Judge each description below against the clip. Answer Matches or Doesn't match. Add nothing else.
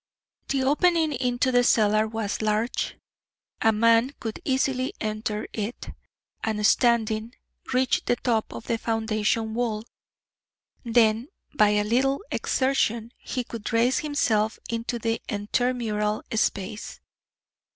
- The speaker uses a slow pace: Matches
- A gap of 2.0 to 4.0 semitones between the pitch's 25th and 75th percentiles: Matches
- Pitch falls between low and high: Doesn't match